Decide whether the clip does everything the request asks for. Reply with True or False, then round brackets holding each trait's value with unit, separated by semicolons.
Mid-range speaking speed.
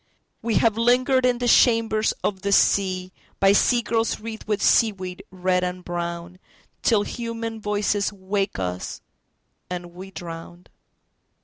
False (125 wpm)